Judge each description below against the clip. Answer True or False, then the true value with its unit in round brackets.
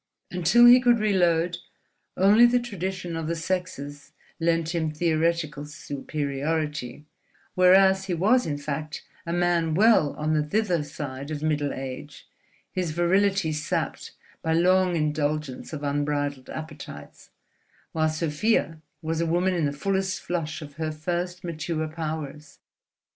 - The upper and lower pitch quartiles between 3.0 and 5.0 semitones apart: True (3.3 semitones)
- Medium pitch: True (160 Hz)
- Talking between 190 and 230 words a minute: False (135 wpm)